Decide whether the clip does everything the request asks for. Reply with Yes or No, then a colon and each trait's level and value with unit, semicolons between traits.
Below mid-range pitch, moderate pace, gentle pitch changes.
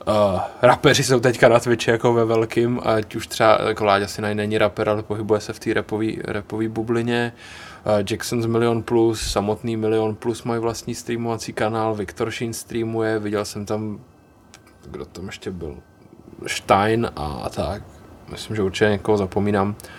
Yes: low, 110 Hz; average, 160 wpm; narrow, 1.7 semitones